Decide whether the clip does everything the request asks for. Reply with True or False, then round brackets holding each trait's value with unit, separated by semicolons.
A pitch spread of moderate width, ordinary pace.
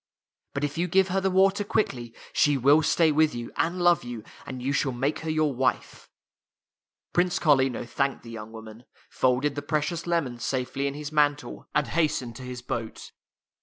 True (4.4 semitones; 190 wpm)